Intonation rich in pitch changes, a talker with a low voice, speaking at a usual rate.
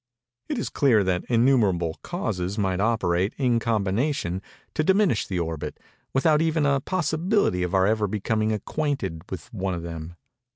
Yes: wide, 7.3 semitones; low, 110 Hz; average, 155 wpm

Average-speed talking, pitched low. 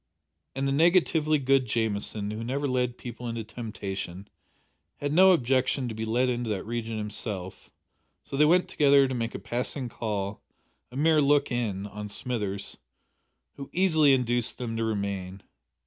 Yes: average, 160 wpm; low, 120 Hz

